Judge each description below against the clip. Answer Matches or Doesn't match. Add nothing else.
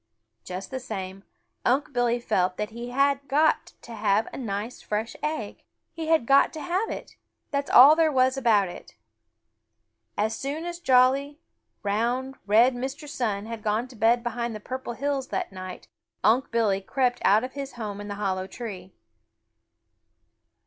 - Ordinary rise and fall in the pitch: Matches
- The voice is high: Matches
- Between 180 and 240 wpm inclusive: Doesn't match